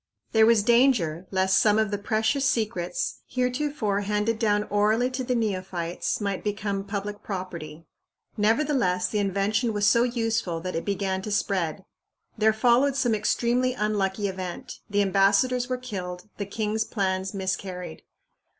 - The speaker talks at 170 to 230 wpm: No, average, 145 wpm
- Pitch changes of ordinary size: Yes, average, 3.2 semitones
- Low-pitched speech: No, high, 210 Hz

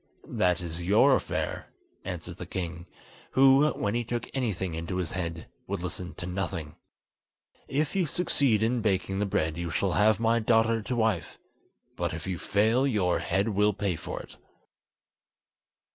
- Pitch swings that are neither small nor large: Yes, average, 4.6 semitones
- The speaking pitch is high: No, low, 100 Hz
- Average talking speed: Yes, average, 160 wpm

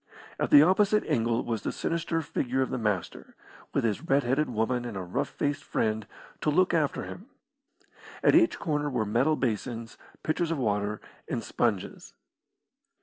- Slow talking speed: No, average, 165 wpm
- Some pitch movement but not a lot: No, wide, 5.8 semitones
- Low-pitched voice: Yes, low, 125 Hz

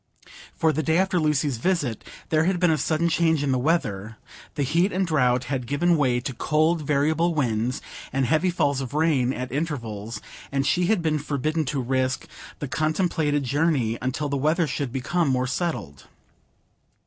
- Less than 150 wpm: No, average, 175 wpm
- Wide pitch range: No, average, 4.0 semitones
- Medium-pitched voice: Yes, medium, 145 Hz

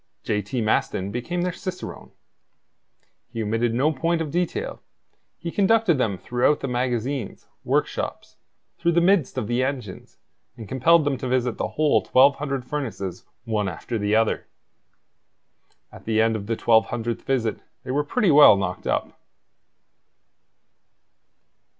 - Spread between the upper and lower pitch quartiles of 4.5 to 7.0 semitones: Yes, average, 5.0 semitones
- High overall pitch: No, low, 125 Hz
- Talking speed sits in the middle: Yes, average, 145 wpm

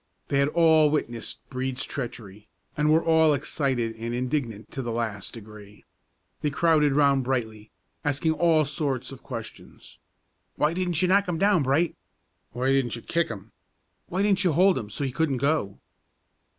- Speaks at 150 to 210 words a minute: Yes, average, 165 wpm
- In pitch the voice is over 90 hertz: Yes, medium, 140 Hz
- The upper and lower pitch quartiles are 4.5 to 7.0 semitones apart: Yes, average, 5.2 semitones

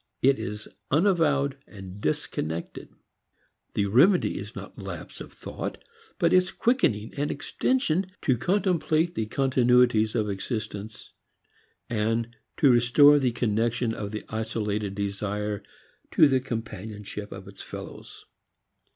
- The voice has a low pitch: Yes, low, 115 Hz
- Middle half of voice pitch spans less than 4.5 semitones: No, average, 5.3 semitones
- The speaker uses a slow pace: Yes, slow, 115 wpm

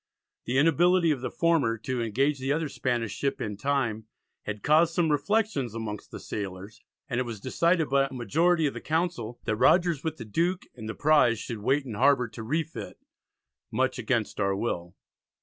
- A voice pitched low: Yes, low, 130 Hz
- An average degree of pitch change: No, wide, 5.9 semitones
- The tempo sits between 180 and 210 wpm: Yes, average, 185 wpm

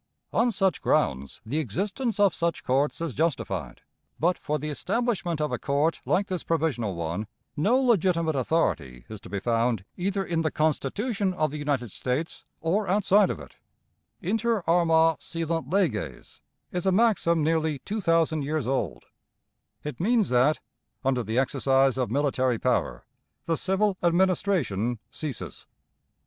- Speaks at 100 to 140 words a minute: No, average, 150 wpm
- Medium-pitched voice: Yes, medium, 160 Hz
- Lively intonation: Yes, wide, 6.5 semitones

